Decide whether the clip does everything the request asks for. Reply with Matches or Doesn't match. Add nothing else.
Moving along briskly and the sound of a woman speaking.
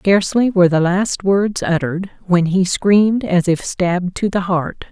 Doesn't match